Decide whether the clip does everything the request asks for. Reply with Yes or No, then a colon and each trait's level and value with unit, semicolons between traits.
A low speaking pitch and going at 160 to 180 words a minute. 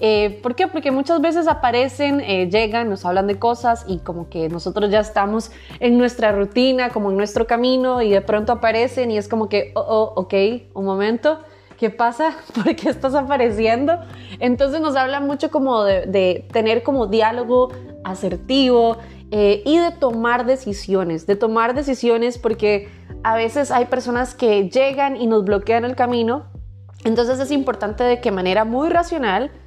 No: high, 235 Hz; average, 170 wpm